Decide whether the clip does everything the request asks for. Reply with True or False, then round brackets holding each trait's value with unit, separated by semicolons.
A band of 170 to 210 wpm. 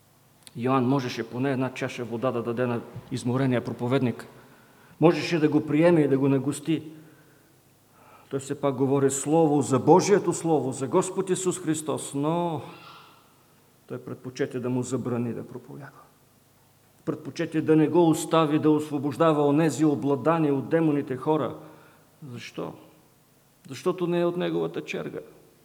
False (135 wpm)